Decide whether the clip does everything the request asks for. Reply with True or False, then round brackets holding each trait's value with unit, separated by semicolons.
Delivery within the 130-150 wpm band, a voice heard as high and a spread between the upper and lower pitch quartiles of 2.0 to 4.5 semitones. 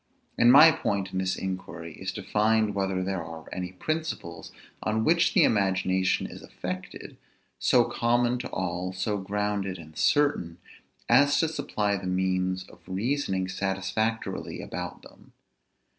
False (145 wpm; 95 Hz; 3.3 semitones)